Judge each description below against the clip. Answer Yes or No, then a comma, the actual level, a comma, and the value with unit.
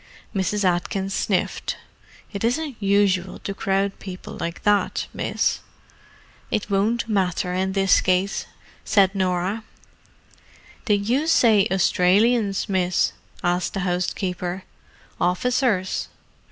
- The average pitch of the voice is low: No, high, 195 Hz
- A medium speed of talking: No, slow, 105 wpm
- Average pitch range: No, narrow, 2.3 semitones